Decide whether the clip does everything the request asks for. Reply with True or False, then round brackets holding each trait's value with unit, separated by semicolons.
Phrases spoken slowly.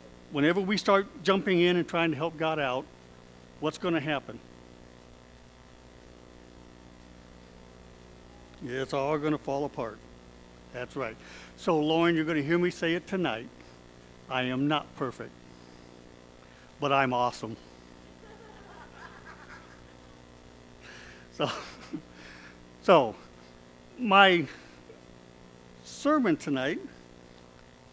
True (95 wpm)